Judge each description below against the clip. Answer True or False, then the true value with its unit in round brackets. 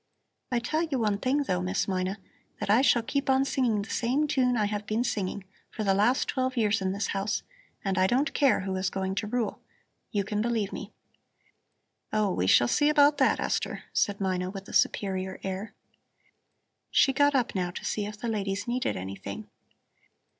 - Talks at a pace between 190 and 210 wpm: True (195 wpm)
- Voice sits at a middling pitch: False (210 Hz)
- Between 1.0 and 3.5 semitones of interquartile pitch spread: False (4.5 semitones)